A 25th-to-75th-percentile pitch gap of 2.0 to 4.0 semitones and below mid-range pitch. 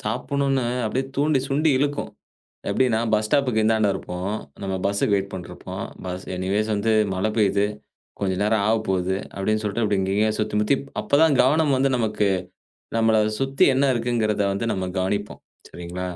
No: average, 4.8 semitones; low, 110 Hz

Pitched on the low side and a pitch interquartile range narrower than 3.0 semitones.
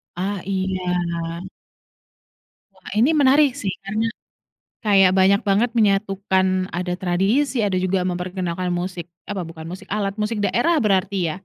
No: high, 190 Hz; narrow, 2.4 semitones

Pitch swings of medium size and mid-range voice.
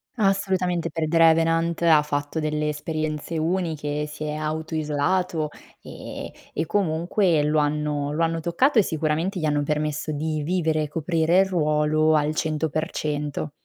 No: narrow, 1.7 semitones; medium, 155 Hz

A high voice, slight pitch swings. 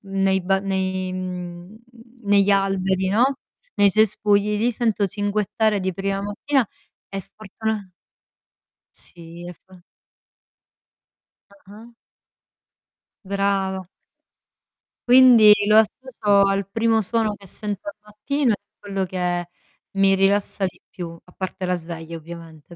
Yes: high, 195 Hz; narrow, 2.3 semitones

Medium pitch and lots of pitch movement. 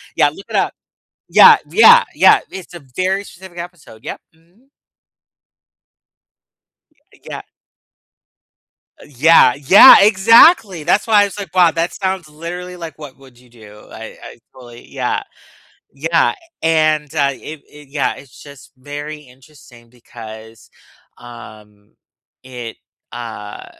Yes: medium, 150 Hz; wide, 6.5 semitones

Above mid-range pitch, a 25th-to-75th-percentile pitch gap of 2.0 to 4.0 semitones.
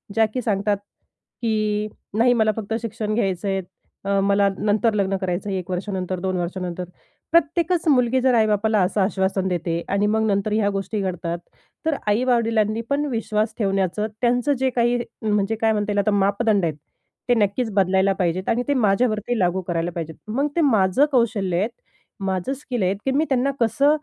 Yes: high, 210 Hz; average, 3.6 semitones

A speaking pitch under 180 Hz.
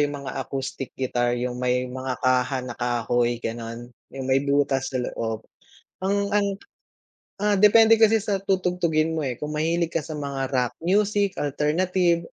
Yes: medium, 140 Hz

